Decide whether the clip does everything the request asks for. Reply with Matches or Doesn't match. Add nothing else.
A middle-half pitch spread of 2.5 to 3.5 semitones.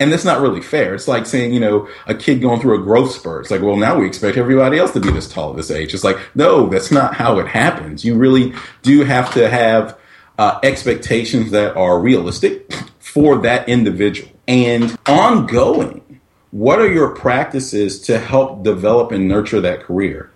Doesn't match